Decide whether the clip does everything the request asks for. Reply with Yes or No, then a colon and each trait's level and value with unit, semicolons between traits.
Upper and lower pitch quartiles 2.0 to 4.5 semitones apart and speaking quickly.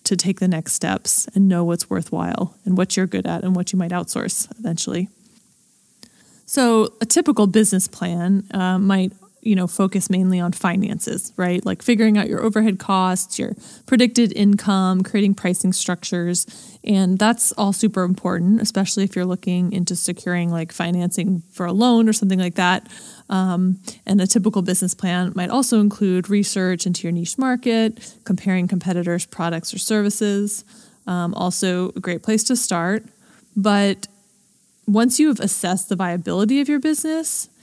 No: average, 3.2 semitones; average, 165 wpm